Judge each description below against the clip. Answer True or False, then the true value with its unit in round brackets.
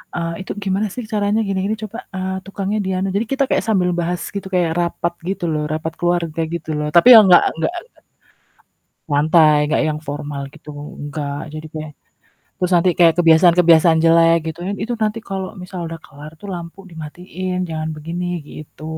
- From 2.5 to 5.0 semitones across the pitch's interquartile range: True (3.2 semitones)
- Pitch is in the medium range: True (170 Hz)